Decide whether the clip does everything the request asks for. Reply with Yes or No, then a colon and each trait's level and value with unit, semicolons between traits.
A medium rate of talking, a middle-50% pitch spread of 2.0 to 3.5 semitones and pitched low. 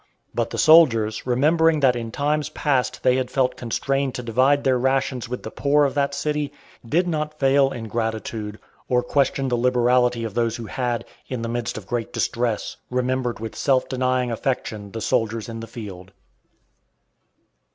Yes: average, 170 wpm; average, 3.0 semitones; low, 125 Hz